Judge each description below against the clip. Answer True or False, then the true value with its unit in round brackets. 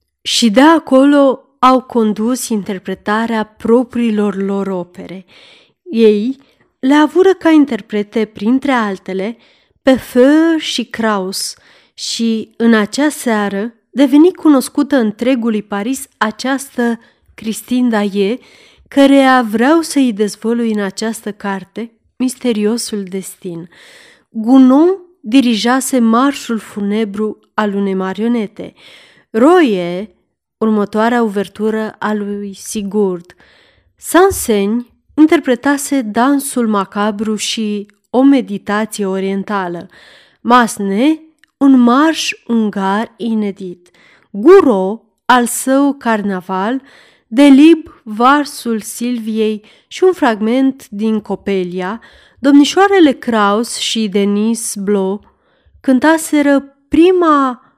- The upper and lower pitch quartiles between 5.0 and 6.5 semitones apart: False (4.6 semitones)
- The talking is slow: True (90 wpm)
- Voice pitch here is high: True (230 Hz)